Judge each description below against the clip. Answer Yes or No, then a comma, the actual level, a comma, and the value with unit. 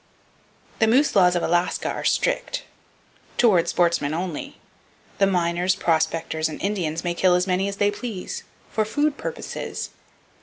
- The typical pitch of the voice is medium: Yes, medium, 180 Hz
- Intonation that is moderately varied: Yes, average, 3.1 semitones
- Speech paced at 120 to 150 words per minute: Yes, average, 140 wpm